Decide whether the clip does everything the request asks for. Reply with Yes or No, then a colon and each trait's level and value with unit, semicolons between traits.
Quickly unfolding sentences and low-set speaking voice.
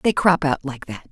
No: fast, 270 wpm; medium, 145 Hz